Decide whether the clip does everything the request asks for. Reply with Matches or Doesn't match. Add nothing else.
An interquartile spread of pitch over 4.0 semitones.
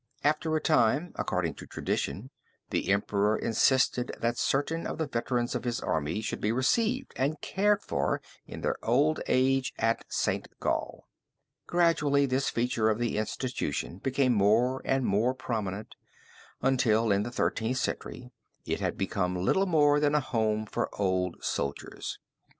Matches